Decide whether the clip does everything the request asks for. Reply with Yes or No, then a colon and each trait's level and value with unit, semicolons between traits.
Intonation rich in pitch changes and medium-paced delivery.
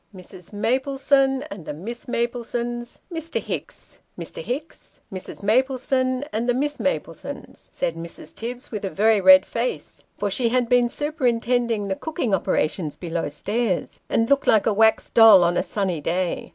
No: average, 4.9 semitones; average, 165 wpm